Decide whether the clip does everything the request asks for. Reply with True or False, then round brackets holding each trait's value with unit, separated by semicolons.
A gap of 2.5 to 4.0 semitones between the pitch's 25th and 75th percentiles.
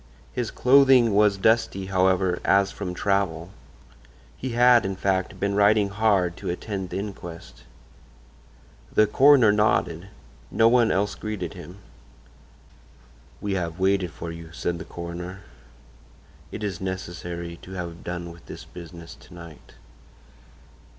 True (3.2 semitones)